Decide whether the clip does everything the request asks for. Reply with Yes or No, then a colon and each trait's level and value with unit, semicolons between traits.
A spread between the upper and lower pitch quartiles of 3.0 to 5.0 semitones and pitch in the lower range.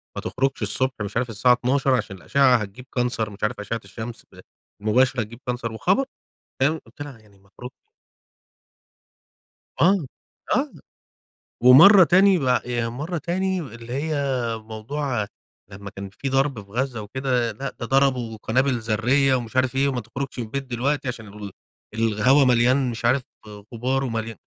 Yes: average, 3.5 semitones; low, 125 Hz